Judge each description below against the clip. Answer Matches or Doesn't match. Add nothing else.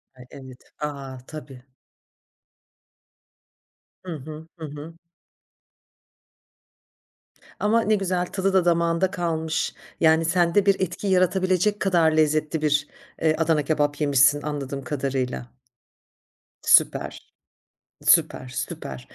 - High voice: Doesn't match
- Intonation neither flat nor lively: Matches